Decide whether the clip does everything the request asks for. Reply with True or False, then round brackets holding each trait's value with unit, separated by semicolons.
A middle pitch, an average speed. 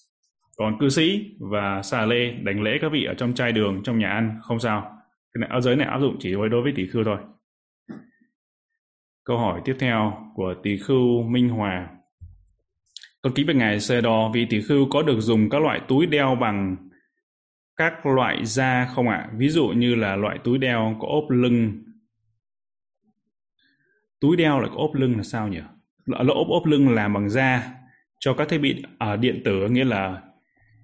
False (120 Hz; 195 wpm)